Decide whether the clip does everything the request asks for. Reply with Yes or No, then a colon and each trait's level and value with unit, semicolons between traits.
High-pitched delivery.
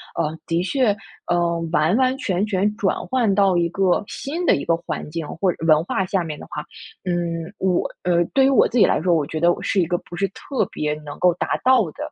No: medium, 175 Hz